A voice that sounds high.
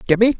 Yes: high, 215 Hz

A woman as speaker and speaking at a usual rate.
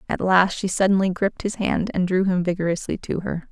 No: female; fast, 220 wpm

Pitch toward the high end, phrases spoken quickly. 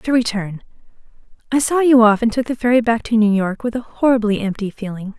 Yes: high, 225 Hz; fast, 220 wpm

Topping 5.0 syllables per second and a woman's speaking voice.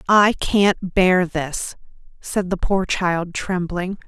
No: 3.0 syllables/s; female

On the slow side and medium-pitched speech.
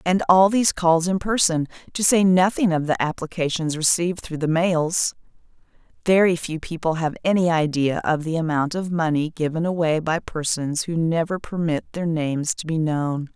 No: average, 175 wpm; medium, 165 Hz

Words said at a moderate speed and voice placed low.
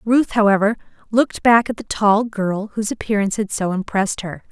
No: average, 185 wpm; high, 210 Hz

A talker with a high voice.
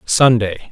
No: low, 115 Hz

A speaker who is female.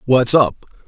No: male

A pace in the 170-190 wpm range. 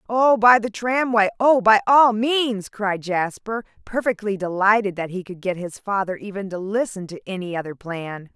Yes: average, 180 wpm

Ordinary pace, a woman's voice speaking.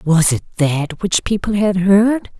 Yes: average, 175 wpm; female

